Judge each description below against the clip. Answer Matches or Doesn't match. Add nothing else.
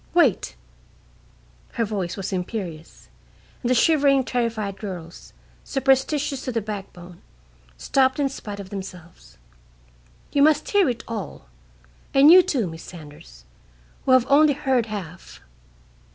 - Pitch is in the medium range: Doesn't match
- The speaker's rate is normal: Doesn't match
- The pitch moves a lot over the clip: Matches